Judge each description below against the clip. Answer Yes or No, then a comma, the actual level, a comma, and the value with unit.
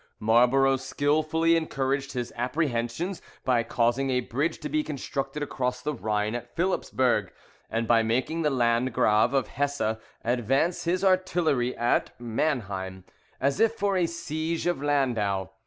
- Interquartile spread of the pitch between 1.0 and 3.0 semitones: No, average, 4.8 semitones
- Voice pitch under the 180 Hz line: Yes, low, 135 Hz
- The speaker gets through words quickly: No, average, 140 wpm